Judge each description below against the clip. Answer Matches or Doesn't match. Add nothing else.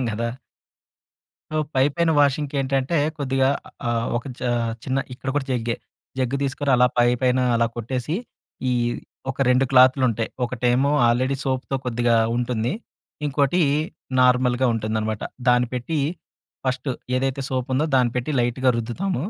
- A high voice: Doesn't match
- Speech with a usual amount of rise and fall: Doesn't match